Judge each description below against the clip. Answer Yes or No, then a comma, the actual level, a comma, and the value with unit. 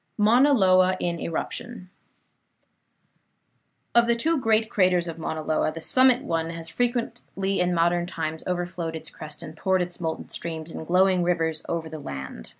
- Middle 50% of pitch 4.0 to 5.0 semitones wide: No, average, 3.4 semitones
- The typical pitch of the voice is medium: Yes, medium, 175 Hz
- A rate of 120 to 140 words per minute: No, average, 160 wpm